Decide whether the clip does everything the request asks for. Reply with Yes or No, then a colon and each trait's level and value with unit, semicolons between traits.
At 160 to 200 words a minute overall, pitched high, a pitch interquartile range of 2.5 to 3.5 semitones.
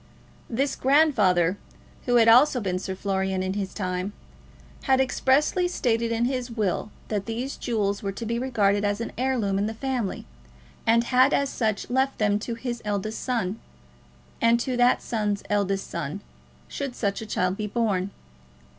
No: average, 165 wpm; high, 225 Hz; average, 3.9 semitones